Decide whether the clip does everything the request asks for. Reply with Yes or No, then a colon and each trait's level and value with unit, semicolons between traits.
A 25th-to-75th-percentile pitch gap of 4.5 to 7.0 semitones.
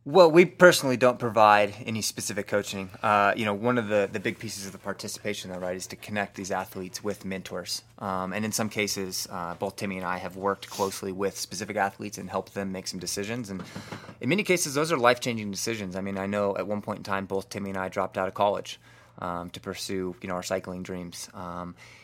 No: narrow, 2.5 semitones